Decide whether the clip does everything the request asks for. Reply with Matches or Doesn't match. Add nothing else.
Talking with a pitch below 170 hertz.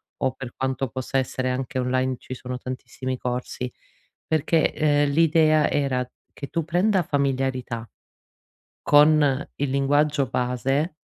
Matches